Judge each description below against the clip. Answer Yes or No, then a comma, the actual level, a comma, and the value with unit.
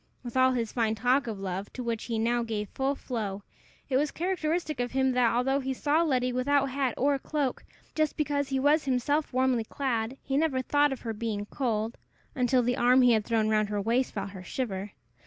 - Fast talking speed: Yes, fast, 210 wpm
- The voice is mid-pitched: No, very high, 250 Hz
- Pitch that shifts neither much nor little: Yes, average, 3.4 semitones